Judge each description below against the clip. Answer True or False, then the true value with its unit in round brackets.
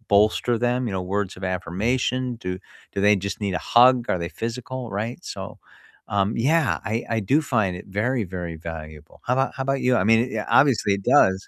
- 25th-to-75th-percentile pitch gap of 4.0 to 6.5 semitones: True (5.2 semitones)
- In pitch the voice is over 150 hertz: False (110 Hz)